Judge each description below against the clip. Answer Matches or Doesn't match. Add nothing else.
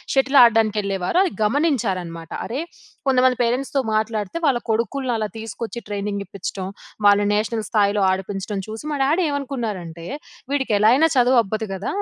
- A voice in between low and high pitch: Doesn't match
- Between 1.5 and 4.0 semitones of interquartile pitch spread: Doesn't match